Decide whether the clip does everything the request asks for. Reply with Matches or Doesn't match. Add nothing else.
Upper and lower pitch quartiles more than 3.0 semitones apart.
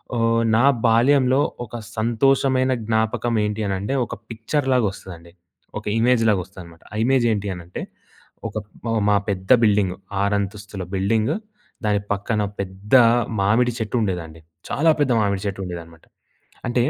Matches